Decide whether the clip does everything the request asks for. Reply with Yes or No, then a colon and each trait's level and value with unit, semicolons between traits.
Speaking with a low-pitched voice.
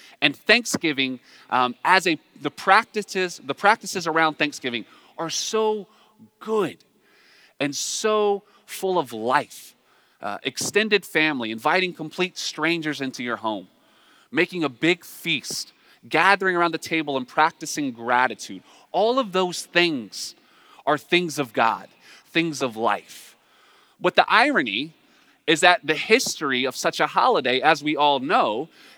No: medium, 160 Hz